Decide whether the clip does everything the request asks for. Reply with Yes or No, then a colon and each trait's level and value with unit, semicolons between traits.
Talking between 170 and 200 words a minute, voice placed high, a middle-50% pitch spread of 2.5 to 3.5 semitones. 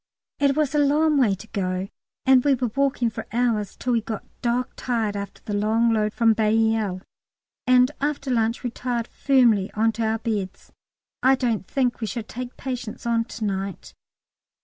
Yes: average, 175 wpm; high, 230 Hz; average, 2.9 semitones